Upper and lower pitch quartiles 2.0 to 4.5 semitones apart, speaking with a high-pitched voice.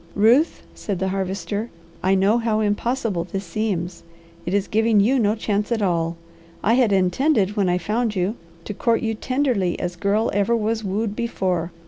Yes: average, 3.2 semitones; high, 205 Hz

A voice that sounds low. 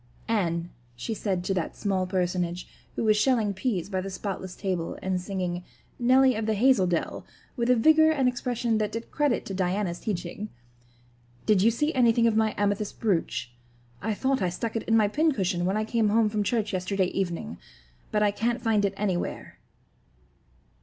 No: high, 210 Hz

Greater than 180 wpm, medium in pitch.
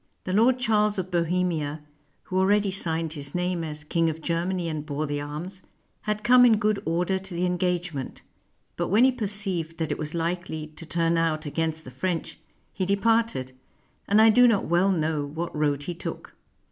Yes: average, 190 wpm; medium, 175 Hz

